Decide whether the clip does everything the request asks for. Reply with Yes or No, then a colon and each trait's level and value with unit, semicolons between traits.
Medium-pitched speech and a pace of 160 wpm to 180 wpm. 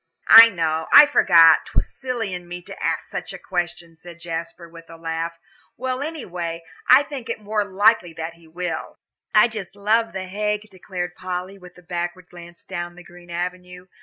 No: medium, 180 Hz; average, 190 wpm